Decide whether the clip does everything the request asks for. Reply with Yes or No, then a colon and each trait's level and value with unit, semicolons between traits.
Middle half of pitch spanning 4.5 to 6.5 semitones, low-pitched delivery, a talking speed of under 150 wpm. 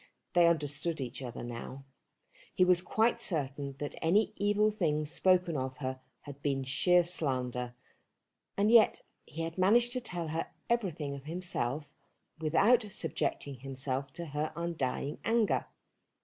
No: average, 5.0 semitones; medium, 160 Hz; average, 140 wpm